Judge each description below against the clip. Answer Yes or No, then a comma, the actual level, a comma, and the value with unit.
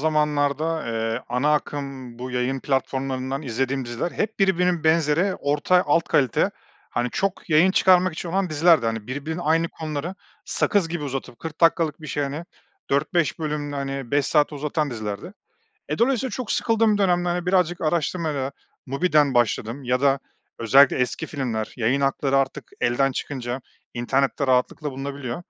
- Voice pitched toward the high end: No, medium, 145 Hz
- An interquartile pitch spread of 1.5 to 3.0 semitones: No, average, 4.1 semitones